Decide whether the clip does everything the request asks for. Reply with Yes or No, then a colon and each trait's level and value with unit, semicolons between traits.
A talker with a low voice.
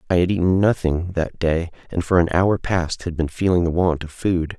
Yes: very low, 85 Hz